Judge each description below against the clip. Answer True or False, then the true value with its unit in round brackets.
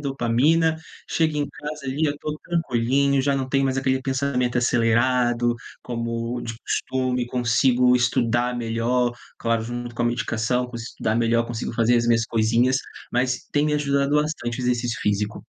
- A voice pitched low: True (125 Hz)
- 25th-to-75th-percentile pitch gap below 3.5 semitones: True (2.5 semitones)